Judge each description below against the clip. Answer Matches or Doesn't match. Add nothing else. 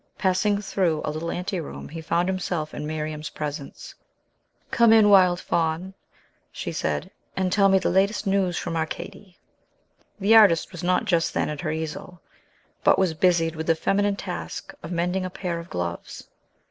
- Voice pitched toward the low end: Doesn't match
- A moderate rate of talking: Matches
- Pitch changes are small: Doesn't match